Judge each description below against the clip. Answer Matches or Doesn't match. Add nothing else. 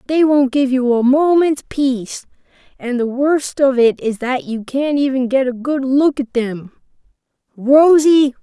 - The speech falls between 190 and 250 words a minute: Doesn't match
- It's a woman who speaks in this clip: Matches